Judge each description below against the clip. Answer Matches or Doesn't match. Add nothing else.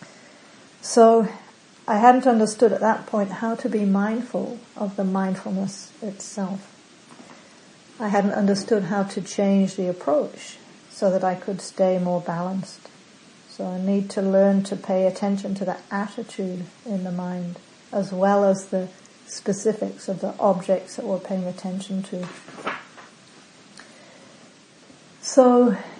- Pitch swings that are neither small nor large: Doesn't match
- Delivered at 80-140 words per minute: Matches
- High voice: Matches